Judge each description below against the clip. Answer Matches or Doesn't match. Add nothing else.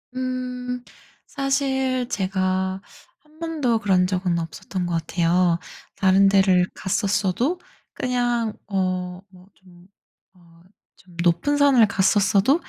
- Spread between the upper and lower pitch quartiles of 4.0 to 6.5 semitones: Matches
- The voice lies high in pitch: Matches